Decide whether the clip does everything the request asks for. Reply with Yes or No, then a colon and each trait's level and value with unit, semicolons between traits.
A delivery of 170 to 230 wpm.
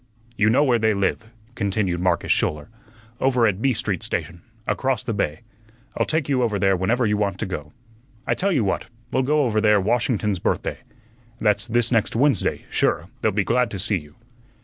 Yes: average, 195 wpm